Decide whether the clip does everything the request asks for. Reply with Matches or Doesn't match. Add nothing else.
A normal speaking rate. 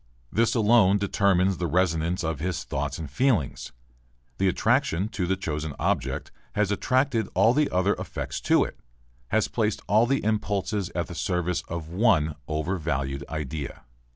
Matches